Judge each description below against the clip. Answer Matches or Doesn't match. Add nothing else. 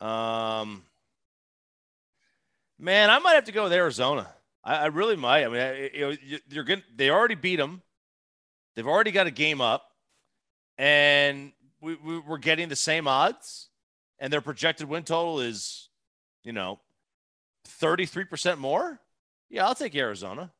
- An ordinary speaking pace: Matches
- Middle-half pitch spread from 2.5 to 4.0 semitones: Doesn't match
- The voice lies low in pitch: Doesn't match